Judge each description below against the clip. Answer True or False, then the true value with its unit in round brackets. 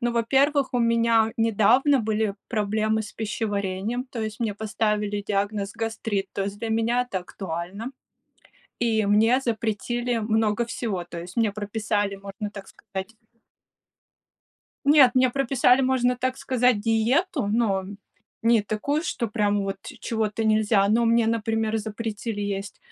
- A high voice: True (220 Hz)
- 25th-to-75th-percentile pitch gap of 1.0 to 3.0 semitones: True (2.4 semitones)